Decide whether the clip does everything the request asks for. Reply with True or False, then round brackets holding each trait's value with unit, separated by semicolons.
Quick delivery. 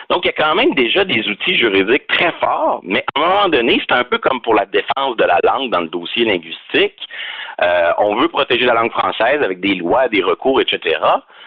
True (230 wpm)